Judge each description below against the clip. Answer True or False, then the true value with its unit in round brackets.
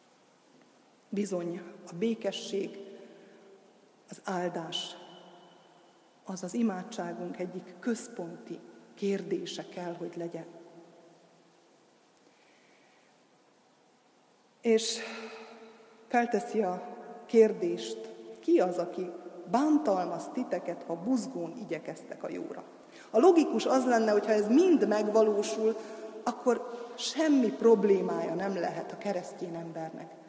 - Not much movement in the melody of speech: False (4.6 semitones)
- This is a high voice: True (205 Hz)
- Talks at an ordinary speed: False (90 wpm)